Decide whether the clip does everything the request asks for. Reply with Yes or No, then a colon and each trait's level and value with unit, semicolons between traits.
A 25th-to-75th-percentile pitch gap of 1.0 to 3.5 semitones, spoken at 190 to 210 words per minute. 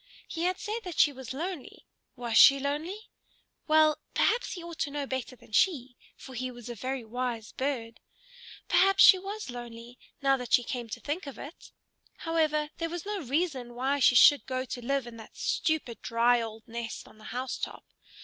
No: average, 4.9 semitones; average, 195 wpm